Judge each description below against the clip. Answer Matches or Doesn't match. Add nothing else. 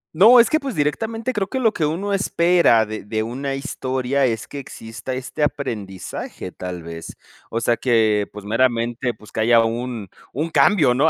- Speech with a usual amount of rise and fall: Doesn't match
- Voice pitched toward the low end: Matches